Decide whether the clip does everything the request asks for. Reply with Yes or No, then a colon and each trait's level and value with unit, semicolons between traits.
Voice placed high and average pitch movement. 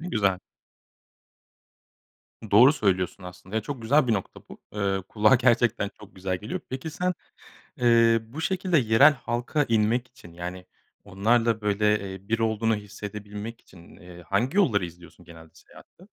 No: low, 110 Hz; average, 3.8 semitones